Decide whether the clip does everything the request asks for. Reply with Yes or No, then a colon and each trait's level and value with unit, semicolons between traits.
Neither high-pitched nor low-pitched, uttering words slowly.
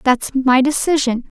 No: very high, 265 Hz; slow, 130 wpm